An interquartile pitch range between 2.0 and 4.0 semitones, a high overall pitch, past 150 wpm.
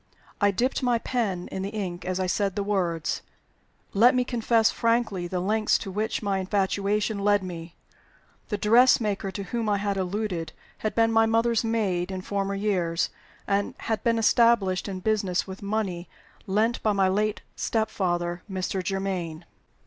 Yes: average, 2.9 semitones; high, 200 Hz; average, 165 wpm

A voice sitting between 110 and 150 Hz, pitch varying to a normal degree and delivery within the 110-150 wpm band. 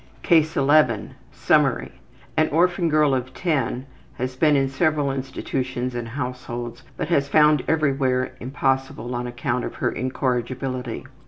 Yes: low, 135 Hz; average, 3.1 semitones; slow, 135 wpm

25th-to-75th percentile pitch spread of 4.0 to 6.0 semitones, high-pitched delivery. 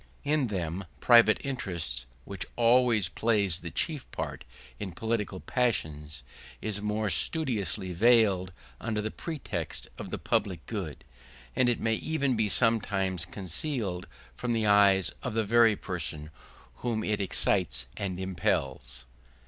No: average, 4.4 semitones; low, 105 Hz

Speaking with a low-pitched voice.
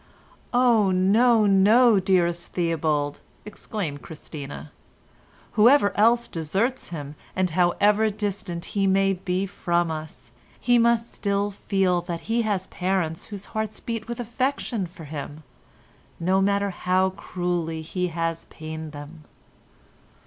No: high, 190 Hz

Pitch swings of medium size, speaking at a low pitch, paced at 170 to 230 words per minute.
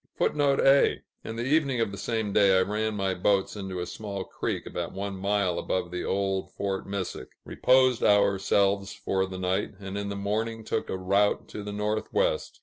No: narrow, 2.2 semitones; low, 100 Hz; average, 190 wpm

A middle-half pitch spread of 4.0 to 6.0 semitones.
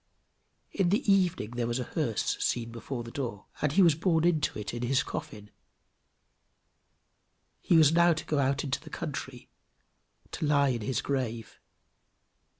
Yes: average, 5.2 semitones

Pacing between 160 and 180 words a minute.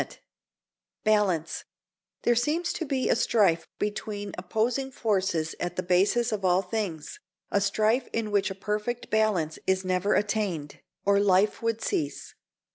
No: average, 145 wpm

